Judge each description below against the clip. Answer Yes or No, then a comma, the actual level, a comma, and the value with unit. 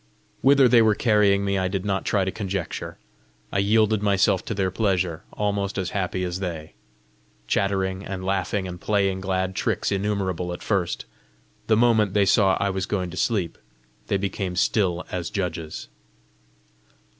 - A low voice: Yes, very low, 95 Hz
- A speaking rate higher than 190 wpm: No, average, 160 wpm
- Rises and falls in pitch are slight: Yes, narrow, 1.7 semitones